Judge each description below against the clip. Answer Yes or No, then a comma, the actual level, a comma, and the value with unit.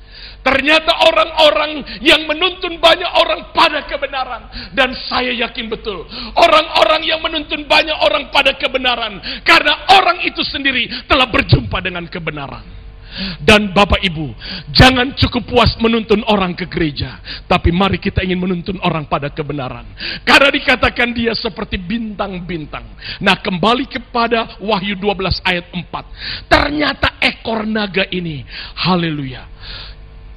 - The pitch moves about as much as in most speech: No, wide, 8.7 semitones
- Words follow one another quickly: No, average, 120 wpm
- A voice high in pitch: Yes, high, 230 Hz